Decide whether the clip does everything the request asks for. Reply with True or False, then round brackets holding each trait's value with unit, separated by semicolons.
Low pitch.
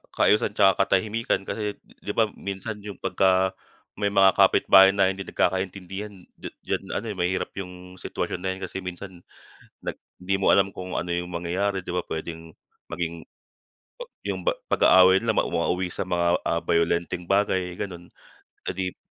True (95 Hz)